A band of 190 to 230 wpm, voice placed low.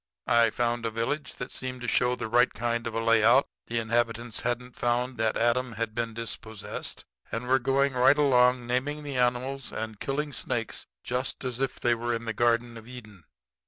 Yes: average, 195 wpm; low, 120 Hz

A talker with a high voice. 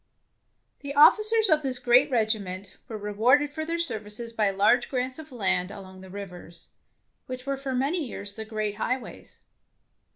Yes: high, 240 Hz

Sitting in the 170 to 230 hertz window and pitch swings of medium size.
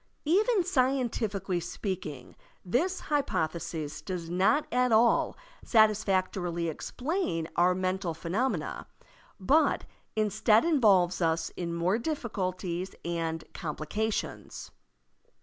No: high, 190 Hz; wide, 6.1 semitones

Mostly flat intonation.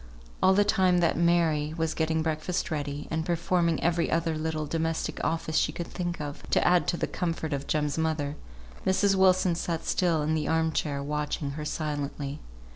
Yes: narrow, 2.2 semitones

